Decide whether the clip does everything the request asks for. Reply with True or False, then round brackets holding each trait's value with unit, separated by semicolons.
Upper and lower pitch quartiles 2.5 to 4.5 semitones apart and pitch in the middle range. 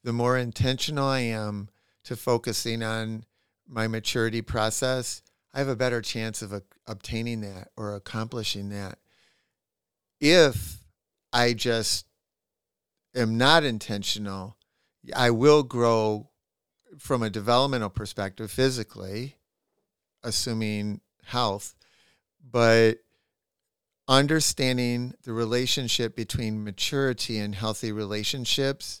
False (2.8 semitones; 115 Hz)